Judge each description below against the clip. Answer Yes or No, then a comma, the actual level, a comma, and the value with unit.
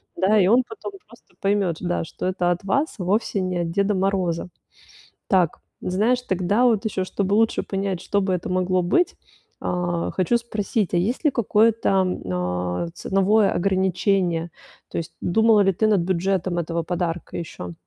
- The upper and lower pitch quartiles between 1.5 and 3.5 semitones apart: Yes, average, 2.8 semitones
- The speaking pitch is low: No, high, 190 Hz